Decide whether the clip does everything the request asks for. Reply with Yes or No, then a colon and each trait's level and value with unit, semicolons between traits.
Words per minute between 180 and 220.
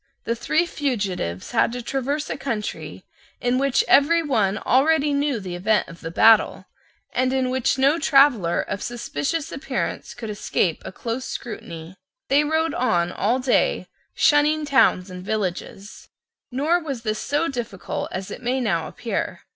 No: average, 155 wpm